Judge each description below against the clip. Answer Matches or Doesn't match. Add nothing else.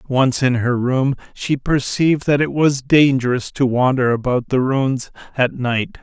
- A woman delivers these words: Doesn't match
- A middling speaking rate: Matches